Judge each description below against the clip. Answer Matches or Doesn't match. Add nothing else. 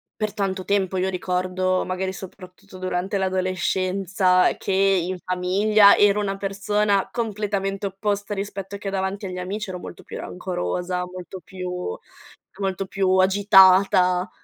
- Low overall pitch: Doesn't match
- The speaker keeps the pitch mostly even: Matches